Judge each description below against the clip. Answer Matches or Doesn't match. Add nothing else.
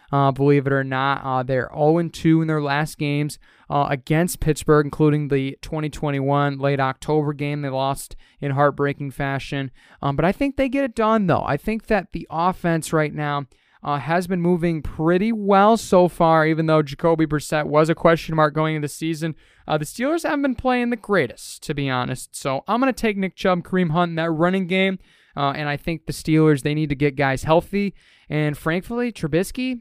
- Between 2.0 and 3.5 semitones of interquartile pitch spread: Doesn't match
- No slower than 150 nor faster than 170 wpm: Doesn't match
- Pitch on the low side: Doesn't match